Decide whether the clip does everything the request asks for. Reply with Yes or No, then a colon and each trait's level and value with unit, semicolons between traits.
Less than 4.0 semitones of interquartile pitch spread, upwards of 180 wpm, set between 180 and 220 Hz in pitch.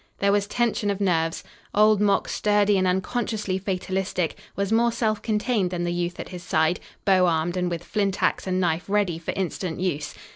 Yes: average, 2.8 semitones; average, 190 wpm; high, 190 Hz